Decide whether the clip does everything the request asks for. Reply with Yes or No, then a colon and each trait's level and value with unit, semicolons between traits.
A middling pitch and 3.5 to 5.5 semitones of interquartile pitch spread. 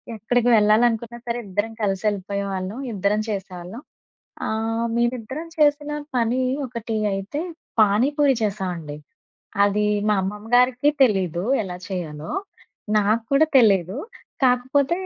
No: high, 215 Hz; average, 3.9 semitones